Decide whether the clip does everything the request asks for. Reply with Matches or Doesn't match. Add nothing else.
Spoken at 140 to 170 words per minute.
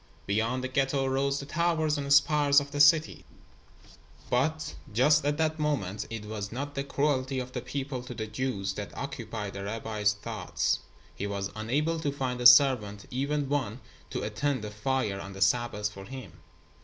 Doesn't match